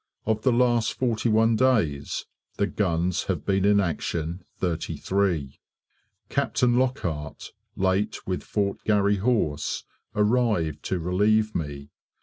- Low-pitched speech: Yes, low, 100 Hz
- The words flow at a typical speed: No, slow, 115 wpm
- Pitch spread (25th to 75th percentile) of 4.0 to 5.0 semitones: Yes, average, 4.6 semitones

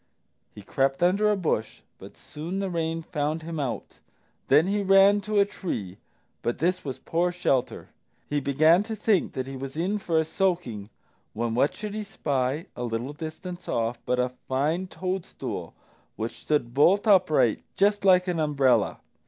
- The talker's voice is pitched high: No, medium, 160 Hz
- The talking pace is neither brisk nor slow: Yes, average, 170 wpm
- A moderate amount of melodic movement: No, wide, 6.1 semitones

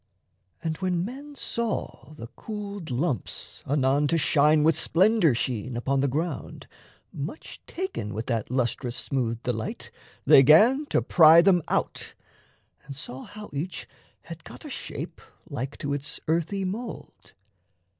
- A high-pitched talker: No, medium, 155 Hz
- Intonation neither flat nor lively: No, wide, 6.3 semitones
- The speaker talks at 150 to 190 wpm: No, average, 140 wpm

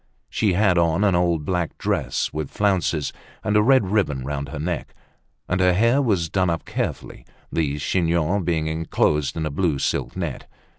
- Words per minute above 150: Yes, average, 180 wpm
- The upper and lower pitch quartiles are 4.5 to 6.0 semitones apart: No, average, 3.8 semitones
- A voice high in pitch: No, very low, 85 Hz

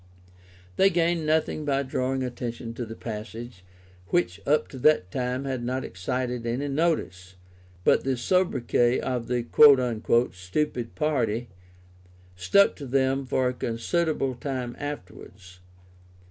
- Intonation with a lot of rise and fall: No, average, 3.4 semitones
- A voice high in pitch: No, low, 125 Hz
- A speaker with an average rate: No, slow, 125 wpm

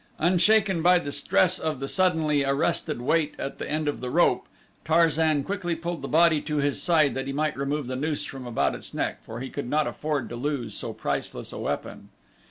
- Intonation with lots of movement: No, average, 3.2 semitones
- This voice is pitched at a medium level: Yes, medium, 150 Hz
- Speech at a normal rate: No, fast, 210 wpm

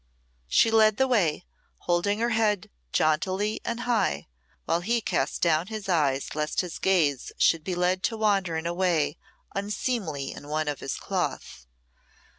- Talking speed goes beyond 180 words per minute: No, average, 160 wpm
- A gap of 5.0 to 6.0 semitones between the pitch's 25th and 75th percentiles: Yes, wide, 5.4 semitones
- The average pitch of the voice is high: No, medium, 180 Hz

